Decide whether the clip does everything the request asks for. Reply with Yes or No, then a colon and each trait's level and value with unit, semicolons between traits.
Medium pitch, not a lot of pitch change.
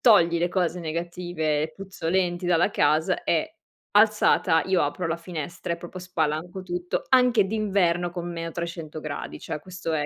Yes: medium, 175 Hz; narrow, 2.0 semitones